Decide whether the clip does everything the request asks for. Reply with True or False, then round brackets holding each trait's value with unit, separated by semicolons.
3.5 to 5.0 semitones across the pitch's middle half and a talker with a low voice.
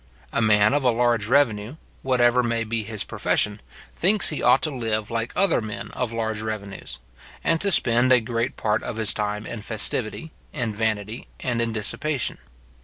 False (2.6 semitones; 115 Hz)